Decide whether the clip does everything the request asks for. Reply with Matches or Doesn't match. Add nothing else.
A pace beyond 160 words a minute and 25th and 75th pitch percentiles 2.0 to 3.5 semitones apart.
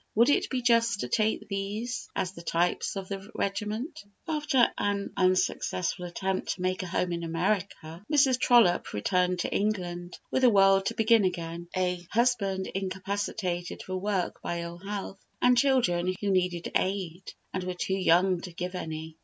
Matches